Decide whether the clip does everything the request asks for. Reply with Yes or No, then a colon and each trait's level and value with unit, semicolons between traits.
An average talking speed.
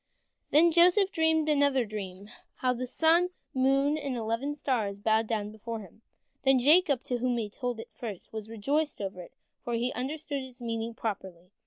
Yes: average, 180 wpm